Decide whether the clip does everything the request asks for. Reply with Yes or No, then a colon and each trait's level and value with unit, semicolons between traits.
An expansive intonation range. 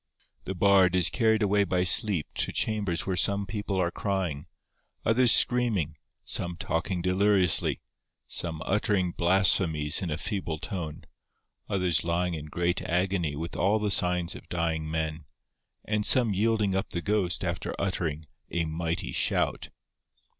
No: average, 3.2 semitones